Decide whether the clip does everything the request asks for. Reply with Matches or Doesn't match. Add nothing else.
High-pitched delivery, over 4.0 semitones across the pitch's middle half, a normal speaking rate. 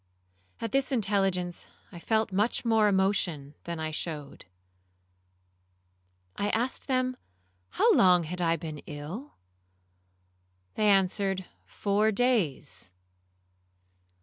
Doesn't match